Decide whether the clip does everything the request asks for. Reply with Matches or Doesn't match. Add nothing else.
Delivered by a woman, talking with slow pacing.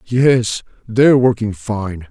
Doesn't match